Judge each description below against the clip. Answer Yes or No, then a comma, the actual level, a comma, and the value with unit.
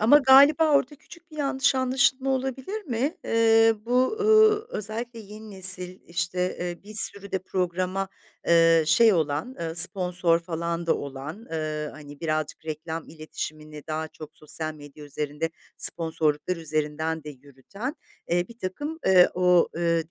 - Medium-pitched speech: Yes, medium, 180 Hz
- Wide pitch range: Yes, wide, 7.1 semitones